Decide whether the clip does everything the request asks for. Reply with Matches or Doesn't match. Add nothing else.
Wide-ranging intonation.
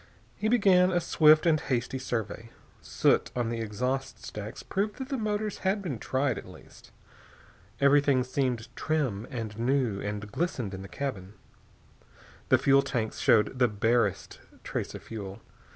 Matches